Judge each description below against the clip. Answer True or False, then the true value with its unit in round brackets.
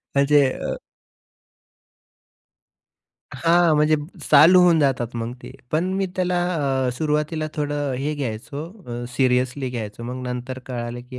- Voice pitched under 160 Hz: True (140 Hz)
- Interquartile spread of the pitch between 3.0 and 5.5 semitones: True (3.7 semitones)